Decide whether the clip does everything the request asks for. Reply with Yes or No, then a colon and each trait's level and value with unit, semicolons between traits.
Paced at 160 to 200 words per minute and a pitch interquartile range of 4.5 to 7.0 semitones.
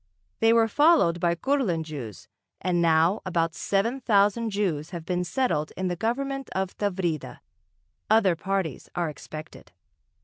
No: average, 140 wpm; average, 5.1 semitones